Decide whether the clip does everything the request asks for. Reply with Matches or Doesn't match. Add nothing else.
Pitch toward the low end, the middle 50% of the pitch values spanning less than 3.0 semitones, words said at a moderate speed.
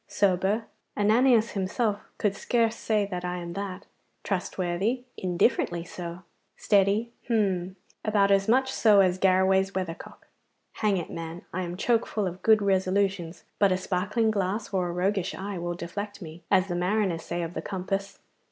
Doesn't match